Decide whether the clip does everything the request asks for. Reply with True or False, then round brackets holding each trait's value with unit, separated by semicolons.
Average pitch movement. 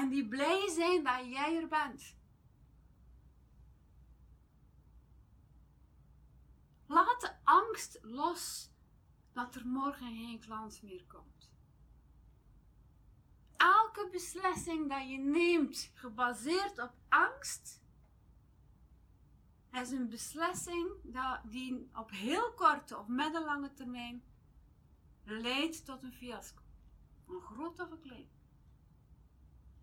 False (6.8 semitones)